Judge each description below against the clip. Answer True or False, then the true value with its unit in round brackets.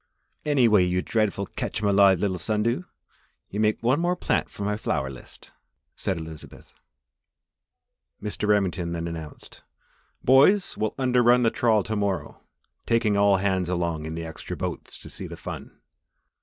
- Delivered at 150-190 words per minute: True (160 wpm)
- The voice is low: True (100 Hz)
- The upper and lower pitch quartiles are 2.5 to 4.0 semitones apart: False (4.5 semitones)